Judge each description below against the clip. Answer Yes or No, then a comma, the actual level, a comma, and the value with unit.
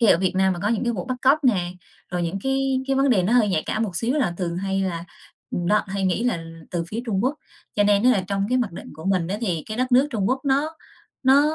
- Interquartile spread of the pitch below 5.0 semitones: No, wide, 5.5 semitones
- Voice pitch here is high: Yes, high, 210 Hz